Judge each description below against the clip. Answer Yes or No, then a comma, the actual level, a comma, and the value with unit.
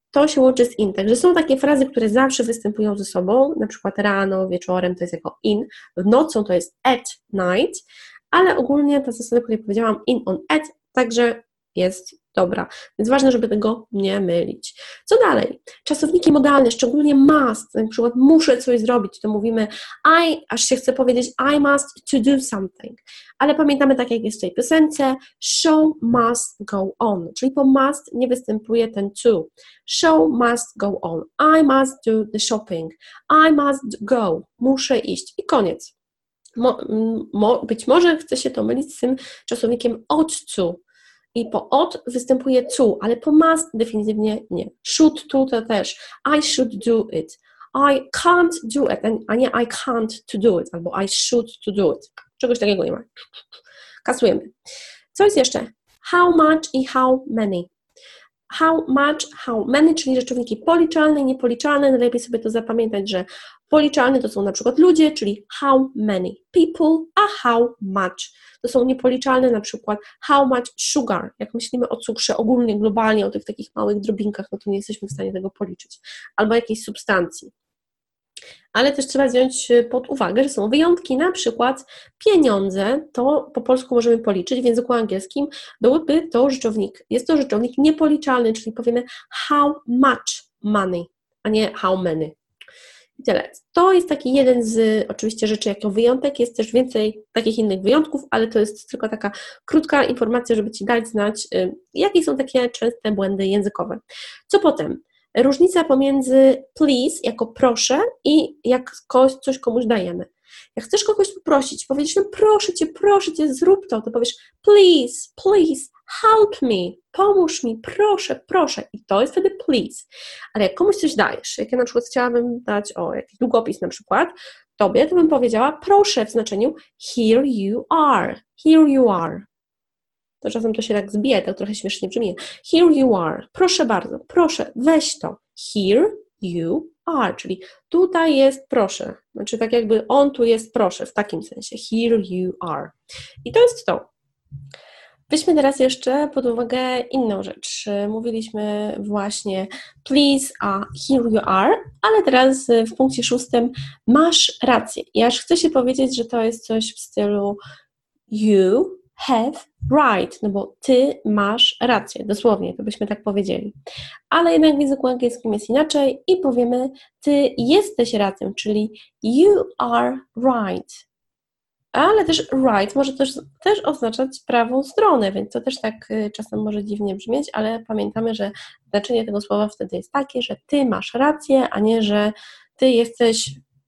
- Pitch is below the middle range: No, high, 245 Hz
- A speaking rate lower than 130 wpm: No, fast, 160 wpm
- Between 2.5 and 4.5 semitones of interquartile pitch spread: No, average, 5.0 semitones